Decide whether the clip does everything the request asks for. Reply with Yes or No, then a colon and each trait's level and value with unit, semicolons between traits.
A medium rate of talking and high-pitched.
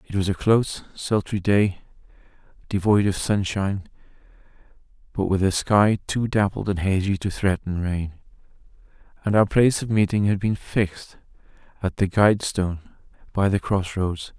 No: average, 150 wpm; low, 100 Hz